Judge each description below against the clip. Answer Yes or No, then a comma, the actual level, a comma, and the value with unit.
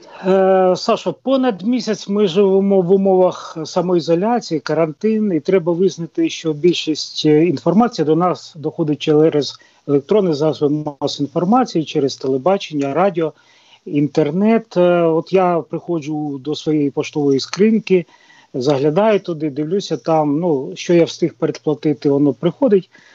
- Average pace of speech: Yes, average, 115 wpm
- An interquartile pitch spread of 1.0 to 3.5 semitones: No, average, 4.0 semitones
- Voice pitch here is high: No, medium, 165 Hz